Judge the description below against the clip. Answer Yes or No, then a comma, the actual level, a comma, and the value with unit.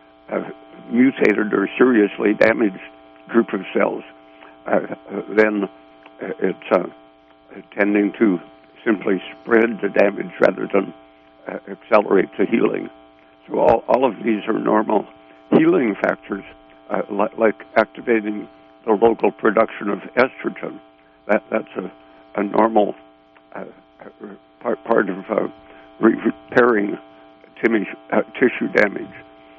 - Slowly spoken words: Yes, slow, 115 wpm